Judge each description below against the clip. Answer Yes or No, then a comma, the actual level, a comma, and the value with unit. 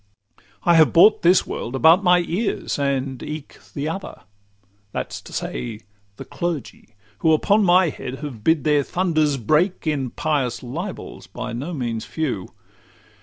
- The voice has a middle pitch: Yes, medium, 150 Hz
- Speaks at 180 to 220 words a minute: No, average, 160 wpm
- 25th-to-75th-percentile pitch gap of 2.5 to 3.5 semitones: No, average, 5.0 semitones